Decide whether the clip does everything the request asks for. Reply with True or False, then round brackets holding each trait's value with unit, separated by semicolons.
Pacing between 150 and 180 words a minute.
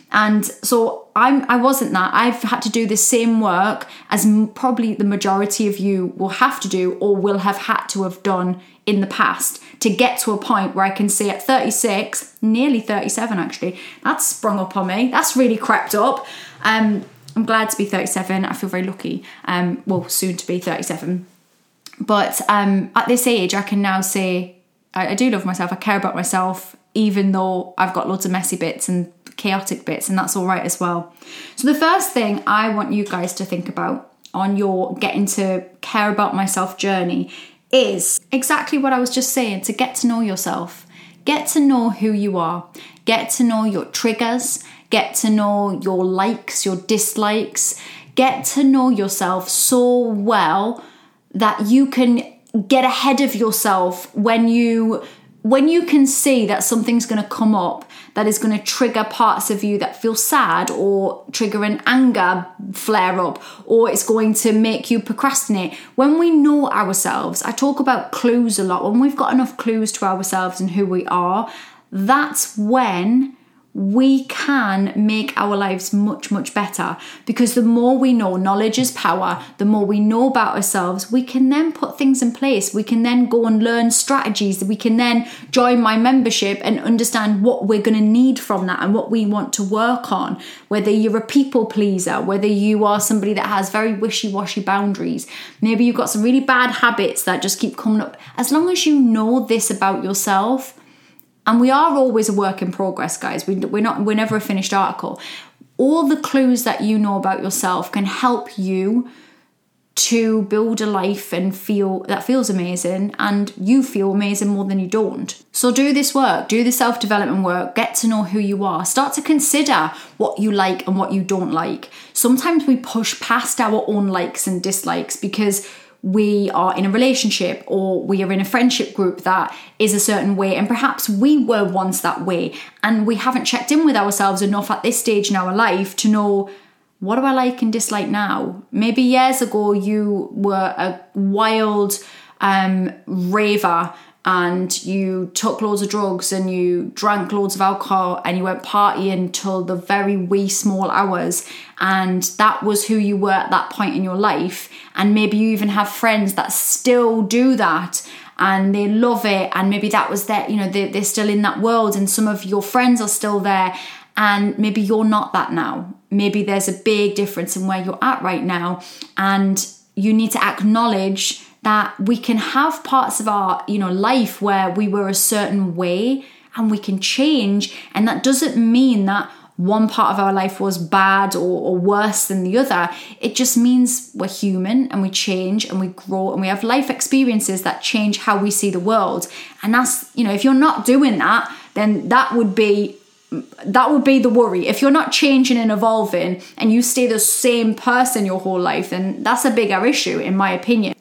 False (195 wpm)